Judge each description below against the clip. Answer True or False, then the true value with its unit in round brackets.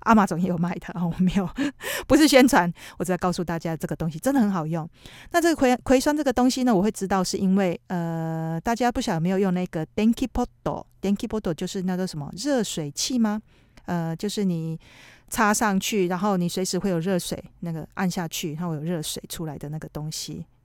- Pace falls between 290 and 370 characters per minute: True (355 characters per minute)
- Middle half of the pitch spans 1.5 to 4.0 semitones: False (4.6 semitones)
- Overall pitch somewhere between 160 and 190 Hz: True (185 Hz)